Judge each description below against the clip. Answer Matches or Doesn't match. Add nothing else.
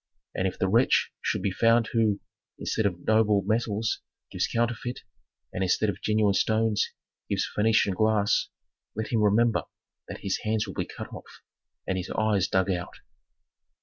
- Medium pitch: Doesn't match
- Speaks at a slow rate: Doesn't match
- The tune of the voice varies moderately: Doesn't match